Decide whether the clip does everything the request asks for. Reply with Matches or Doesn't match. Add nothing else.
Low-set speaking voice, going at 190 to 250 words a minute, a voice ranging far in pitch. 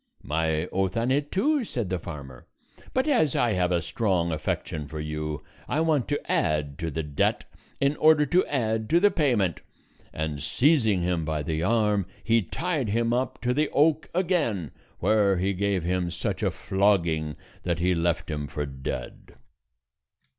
Doesn't match